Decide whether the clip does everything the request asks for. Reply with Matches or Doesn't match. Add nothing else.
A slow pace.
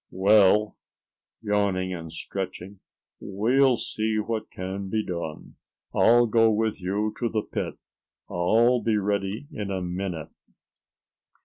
Matches